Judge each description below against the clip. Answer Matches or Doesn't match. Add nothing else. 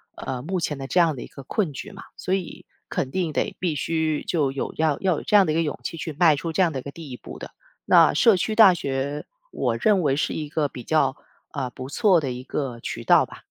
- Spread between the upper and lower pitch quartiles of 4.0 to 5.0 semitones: Matches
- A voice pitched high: Doesn't match